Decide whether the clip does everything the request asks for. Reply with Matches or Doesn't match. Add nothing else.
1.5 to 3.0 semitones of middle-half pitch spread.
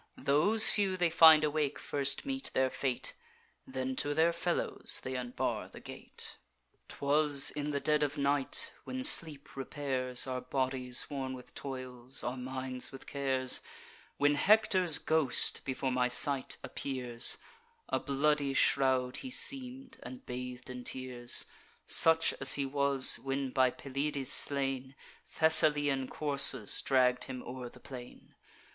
Matches